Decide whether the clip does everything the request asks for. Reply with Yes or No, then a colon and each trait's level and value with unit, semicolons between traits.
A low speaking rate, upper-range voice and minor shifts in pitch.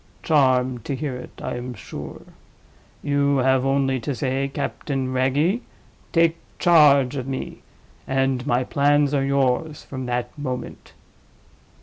No: slow, 125 wpm; low, 135 Hz; narrow, 1.9 semitones